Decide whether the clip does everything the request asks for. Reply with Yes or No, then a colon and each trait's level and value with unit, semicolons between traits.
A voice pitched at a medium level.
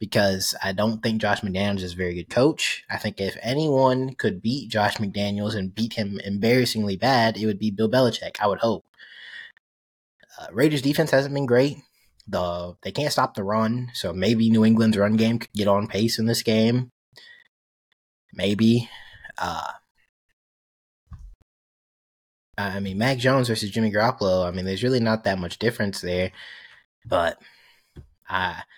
No: low, 110 Hz